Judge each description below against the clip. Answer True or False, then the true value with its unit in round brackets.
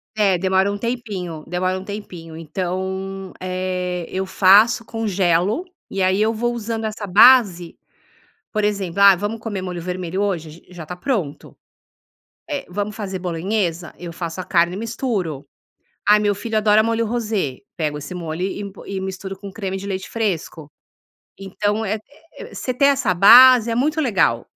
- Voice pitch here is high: True (195 Hz)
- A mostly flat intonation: False (3.4 semitones)